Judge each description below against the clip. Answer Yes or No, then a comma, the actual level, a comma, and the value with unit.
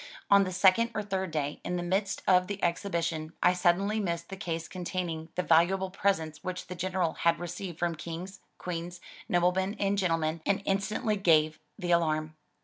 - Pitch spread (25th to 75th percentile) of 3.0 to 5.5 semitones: No, narrow, 2.5 semitones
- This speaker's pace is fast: No, average, 175 wpm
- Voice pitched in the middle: Yes, medium, 180 Hz